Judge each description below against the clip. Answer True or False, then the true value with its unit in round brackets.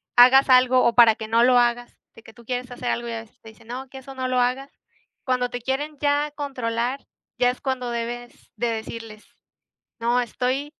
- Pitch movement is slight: True (1.9 semitones)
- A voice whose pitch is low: False (245 Hz)